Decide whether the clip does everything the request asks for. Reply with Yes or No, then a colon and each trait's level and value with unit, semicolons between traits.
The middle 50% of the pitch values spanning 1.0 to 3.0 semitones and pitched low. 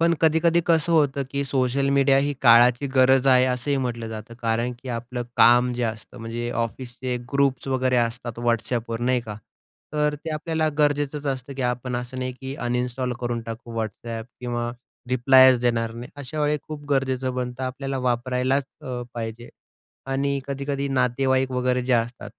Yes: narrow, 2.4 semitones; low, 125 Hz